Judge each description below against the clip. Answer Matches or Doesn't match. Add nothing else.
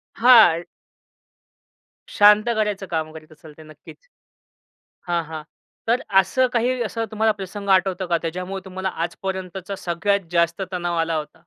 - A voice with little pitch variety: Doesn't match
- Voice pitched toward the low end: Doesn't match